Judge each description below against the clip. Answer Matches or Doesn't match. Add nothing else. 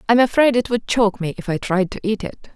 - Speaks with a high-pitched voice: Matches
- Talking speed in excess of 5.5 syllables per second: Matches